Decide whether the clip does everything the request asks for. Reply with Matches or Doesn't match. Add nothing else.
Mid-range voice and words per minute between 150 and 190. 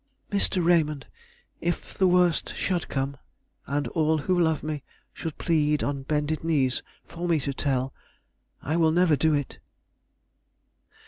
Doesn't match